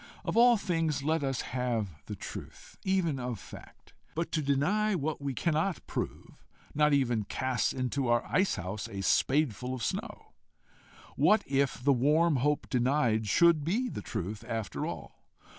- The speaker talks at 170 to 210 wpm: No, average, 160 wpm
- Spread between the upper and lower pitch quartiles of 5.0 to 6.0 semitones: Yes, average, 5.3 semitones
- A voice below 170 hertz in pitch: Yes, medium, 140 Hz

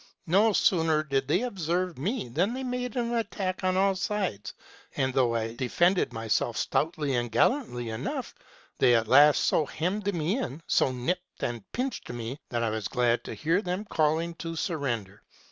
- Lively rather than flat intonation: Yes, wide, 7.8 semitones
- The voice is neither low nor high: Yes, medium, 160 Hz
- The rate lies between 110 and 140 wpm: No, average, 175 wpm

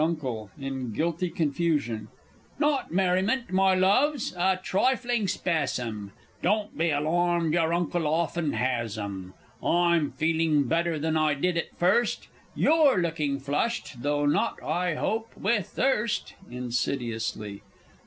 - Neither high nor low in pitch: Yes, medium, 165 Hz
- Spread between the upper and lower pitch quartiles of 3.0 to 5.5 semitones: Yes, average, 5.1 semitones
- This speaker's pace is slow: Yes, slow, 125 wpm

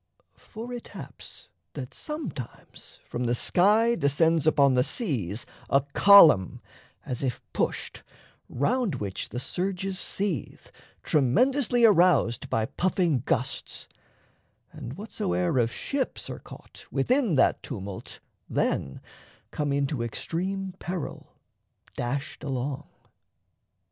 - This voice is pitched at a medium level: Yes, medium, 150 Hz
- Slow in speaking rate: Yes, slow, 110 wpm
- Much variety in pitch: Yes, wide, 8.3 semitones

